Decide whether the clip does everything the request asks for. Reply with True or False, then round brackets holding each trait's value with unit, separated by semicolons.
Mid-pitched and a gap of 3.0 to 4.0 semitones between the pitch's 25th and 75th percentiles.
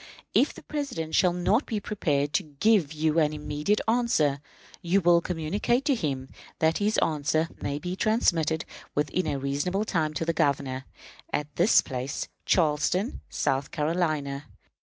False (160 Hz; 4.5 semitones)